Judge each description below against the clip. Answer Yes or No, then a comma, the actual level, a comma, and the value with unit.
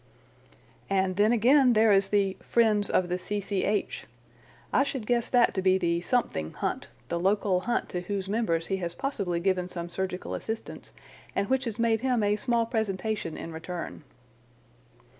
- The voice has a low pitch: No, high, 200 Hz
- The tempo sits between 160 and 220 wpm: Yes, average, 165 wpm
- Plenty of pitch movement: No, average, 3.8 semitones